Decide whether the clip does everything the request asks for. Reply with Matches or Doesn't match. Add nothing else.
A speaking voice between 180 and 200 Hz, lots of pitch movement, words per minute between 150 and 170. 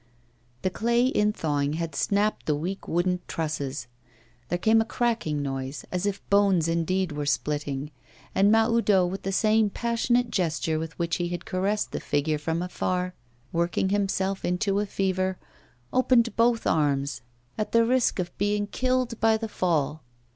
Doesn't match